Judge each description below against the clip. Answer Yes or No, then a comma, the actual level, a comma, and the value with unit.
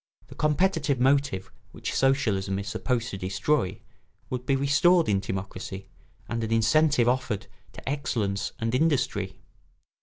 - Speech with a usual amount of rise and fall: No, wide, 6.1 semitones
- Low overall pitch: Yes, low, 120 Hz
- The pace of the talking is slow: Yes, slow, 130 wpm